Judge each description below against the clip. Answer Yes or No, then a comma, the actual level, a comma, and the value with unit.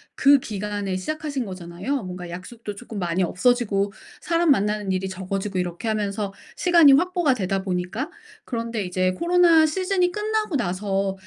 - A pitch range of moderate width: No, wide, 7.3 semitones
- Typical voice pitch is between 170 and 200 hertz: No, high, 210 Hz